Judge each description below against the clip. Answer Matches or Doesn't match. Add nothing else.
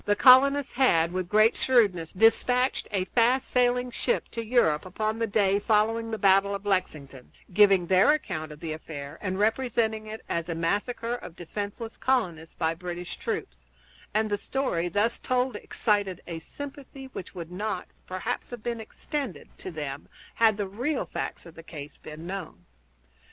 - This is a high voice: Matches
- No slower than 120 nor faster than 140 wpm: Doesn't match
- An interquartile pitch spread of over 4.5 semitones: Matches